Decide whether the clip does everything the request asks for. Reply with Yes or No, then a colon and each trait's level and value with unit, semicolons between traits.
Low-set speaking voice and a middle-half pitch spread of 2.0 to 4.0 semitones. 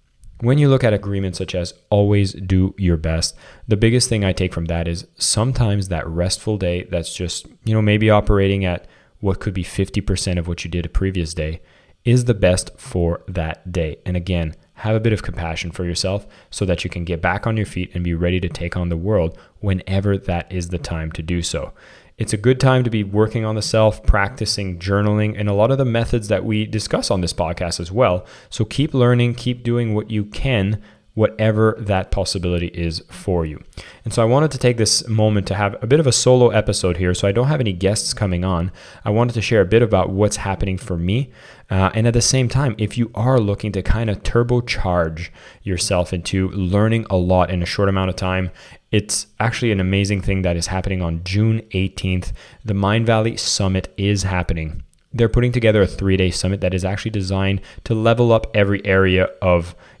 Yes: low, 100 Hz; average, 3.5 semitones